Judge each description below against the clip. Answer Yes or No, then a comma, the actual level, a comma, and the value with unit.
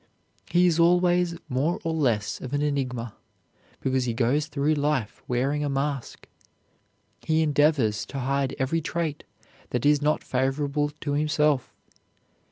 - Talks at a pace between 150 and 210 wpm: No, average, 140 wpm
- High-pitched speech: No, medium, 145 Hz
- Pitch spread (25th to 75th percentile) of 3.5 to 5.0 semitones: No, average, 2.7 semitones